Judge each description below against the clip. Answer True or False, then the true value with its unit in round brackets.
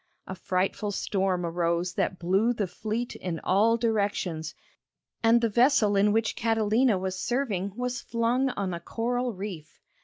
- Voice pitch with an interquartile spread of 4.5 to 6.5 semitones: False (4.0 semitones)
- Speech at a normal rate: True (150 wpm)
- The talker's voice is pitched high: True (205 Hz)